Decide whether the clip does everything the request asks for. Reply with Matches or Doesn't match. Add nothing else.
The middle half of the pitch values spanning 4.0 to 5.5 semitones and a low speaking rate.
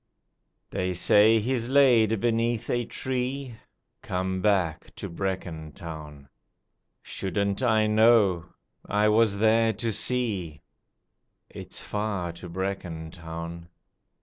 Matches